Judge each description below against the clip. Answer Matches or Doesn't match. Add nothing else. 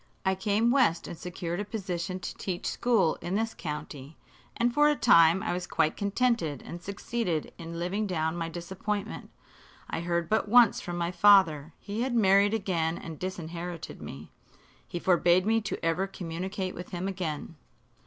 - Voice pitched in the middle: Matches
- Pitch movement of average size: Matches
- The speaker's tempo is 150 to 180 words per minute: Matches